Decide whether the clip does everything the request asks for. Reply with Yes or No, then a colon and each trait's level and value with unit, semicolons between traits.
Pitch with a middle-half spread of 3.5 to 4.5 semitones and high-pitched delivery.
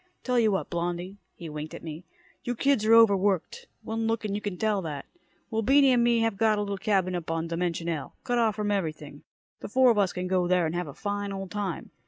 Yes: average, 4.2 semitones; high, 200 Hz